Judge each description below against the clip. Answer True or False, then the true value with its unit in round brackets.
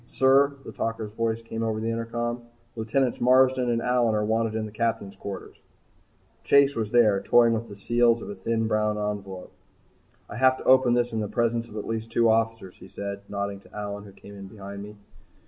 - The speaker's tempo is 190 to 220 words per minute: True (205 wpm)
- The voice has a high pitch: False (115 Hz)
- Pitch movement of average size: False (2.3 semitones)